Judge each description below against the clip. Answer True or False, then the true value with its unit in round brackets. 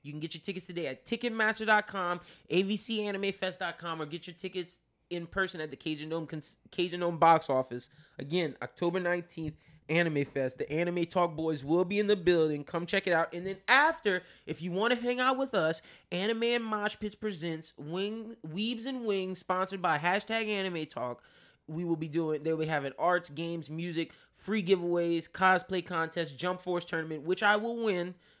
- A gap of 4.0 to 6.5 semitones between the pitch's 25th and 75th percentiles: False (3.5 semitones)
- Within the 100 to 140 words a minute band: False (180 wpm)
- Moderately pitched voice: True (175 Hz)